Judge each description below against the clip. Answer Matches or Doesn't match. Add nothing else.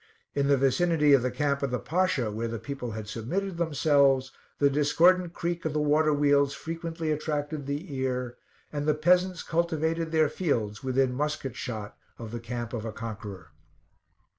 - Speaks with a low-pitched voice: Doesn't match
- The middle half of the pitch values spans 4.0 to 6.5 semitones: Matches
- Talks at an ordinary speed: Matches